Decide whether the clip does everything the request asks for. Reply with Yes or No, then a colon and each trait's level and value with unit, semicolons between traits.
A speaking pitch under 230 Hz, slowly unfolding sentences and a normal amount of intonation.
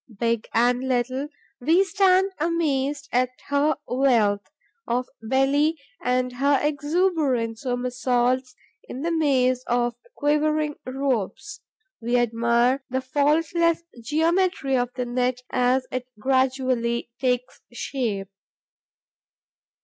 No: very high, 260 Hz; slow, 105 wpm; average, 3.2 semitones